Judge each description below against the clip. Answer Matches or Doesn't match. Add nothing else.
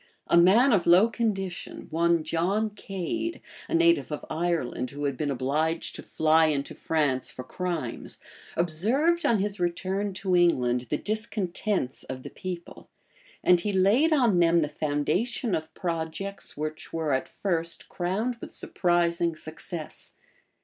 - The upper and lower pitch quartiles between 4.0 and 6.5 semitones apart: Matches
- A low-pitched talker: Doesn't match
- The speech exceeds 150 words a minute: Doesn't match